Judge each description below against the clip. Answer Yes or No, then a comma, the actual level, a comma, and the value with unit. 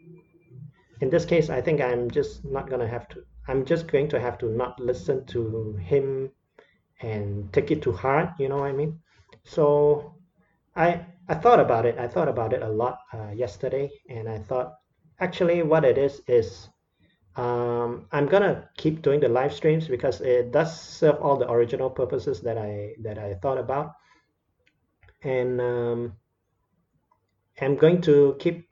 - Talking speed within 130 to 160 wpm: No, average, 170 wpm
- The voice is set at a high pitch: No, low, 135 Hz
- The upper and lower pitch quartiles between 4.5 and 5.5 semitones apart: Yes, average, 4.9 semitones